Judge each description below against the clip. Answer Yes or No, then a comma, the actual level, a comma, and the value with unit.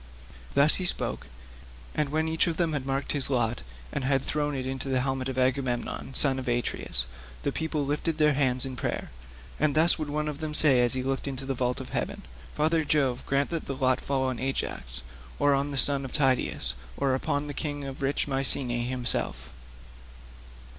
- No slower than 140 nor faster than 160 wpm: No, average, 200 wpm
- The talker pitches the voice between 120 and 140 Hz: Yes, low, 135 Hz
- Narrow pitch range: Yes, narrow, 2.2 semitones